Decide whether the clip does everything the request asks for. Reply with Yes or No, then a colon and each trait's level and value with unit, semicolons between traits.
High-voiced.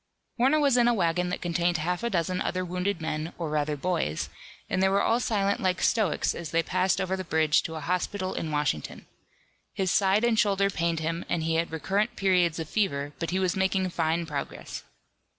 No: medium, 180 Hz